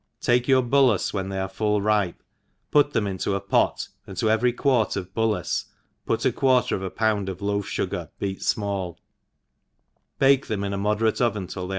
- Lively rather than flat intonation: No, average, 3.5 semitones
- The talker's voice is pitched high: No, low, 105 Hz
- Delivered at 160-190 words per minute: No, average, 200 wpm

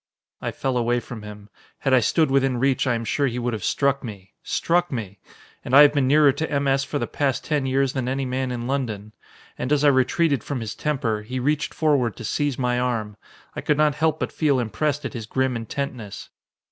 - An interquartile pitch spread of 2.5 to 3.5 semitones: Yes, average, 3.2 semitones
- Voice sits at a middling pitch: No, low, 130 Hz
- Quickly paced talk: Yes, fast, 225 wpm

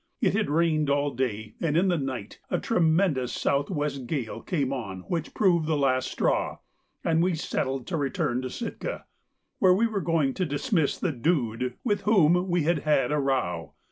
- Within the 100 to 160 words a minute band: No, average, 185 wpm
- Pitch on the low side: No, medium, 150 Hz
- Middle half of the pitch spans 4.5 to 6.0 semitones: Yes, average, 5.1 semitones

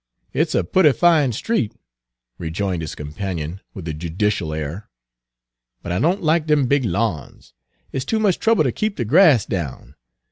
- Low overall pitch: Yes, low, 105 Hz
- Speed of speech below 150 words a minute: No, average, 165 wpm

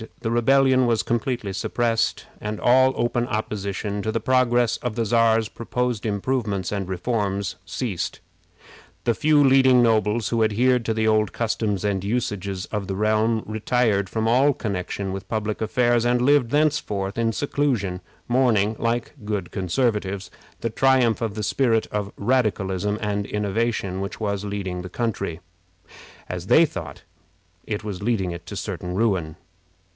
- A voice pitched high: No, low, 110 Hz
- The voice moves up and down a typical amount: Yes, average, 3.2 semitones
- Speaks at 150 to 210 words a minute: No, average, 140 wpm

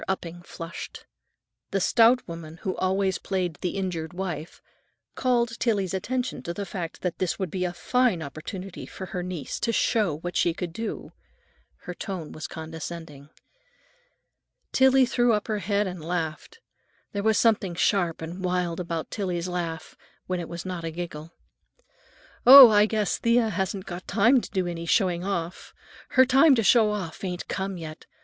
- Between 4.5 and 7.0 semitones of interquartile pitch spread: No, average, 3.8 semitones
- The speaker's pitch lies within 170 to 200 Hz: Yes, medium, 185 Hz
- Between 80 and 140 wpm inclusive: No, average, 165 wpm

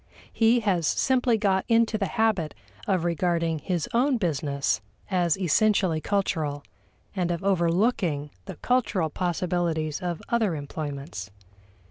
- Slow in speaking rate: Yes, slow, 120 wpm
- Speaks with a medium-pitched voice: Yes, medium, 175 Hz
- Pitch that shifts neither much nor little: Yes, average, 4.9 semitones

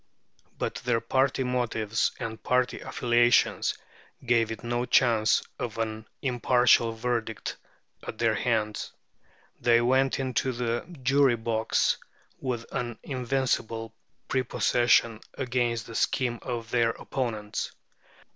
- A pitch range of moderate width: No, narrow, 1.8 semitones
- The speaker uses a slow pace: Yes, slow, 110 wpm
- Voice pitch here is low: Yes, low, 120 Hz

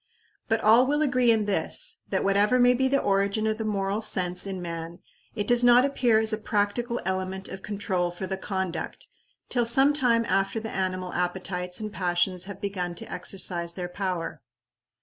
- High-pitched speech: Yes, high, 200 Hz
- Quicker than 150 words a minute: Yes, average, 185 wpm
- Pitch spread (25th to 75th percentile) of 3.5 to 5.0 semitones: Yes, average, 4.0 semitones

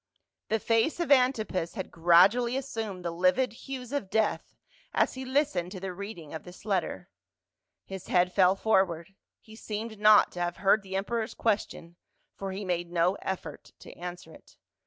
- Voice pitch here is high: Yes, high, 195 Hz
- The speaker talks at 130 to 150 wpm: No, average, 170 wpm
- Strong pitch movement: No, average, 4.0 semitones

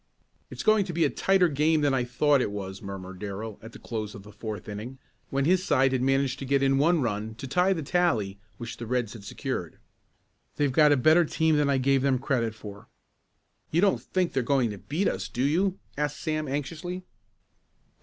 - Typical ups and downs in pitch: No, wide, 5.7 semitones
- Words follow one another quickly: Yes, fast, 215 wpm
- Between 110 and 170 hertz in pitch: Yes, low, 135 Hz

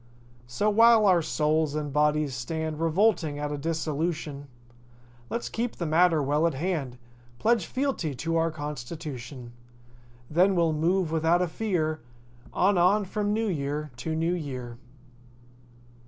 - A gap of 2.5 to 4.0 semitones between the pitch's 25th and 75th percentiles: Yes, average, 3.5 semitones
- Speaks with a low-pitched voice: No, medium, 160 Hz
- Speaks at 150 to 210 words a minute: No, average, 140 wpm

